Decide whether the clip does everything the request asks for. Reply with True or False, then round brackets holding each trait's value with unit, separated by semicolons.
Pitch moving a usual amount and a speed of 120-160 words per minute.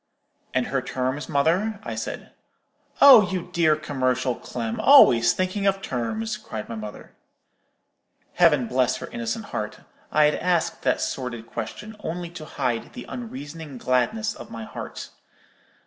False (6.9 semitones; 145 wpm)